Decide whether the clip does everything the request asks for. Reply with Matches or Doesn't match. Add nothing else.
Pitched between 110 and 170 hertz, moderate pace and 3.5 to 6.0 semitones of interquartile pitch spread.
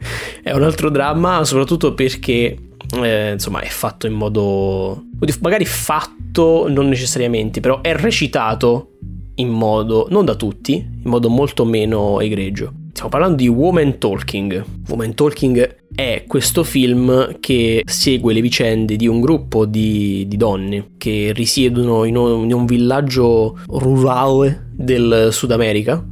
Matches